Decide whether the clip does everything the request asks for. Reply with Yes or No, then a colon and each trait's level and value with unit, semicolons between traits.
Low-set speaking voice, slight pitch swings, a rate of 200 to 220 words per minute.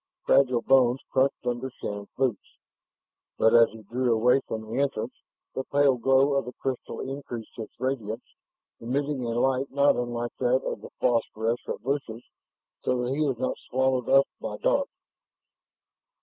No: low, 125 Hz; narrow, 2.3 semitones; average, 155 wpm